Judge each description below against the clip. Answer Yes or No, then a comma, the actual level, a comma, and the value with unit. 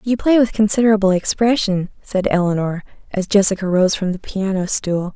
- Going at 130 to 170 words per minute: Yes, average, 165 wpm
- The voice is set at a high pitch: Yes, high, 195 Hz